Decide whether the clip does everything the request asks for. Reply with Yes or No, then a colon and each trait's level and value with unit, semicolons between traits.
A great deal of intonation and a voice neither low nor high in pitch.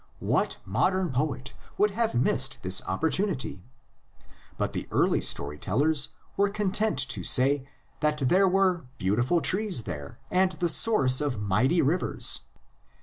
Yes: wide, 7.2 semitones; medium, 150 Hz